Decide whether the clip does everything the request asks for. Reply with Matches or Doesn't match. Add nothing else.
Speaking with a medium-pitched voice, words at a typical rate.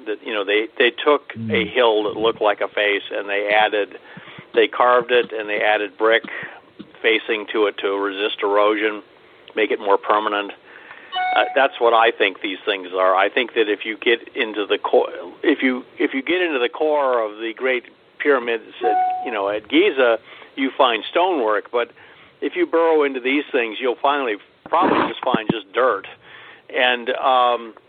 Doesn't match